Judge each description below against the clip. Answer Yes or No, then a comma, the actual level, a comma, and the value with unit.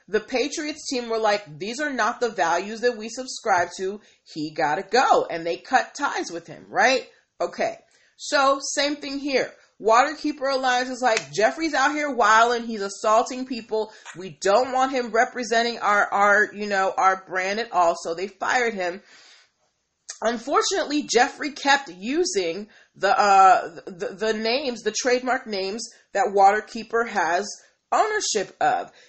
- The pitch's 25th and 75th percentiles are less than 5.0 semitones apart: No, wide, 5.4 semitones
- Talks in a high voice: Yes, high, 230 Hz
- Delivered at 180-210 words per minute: No, average, 155 wpm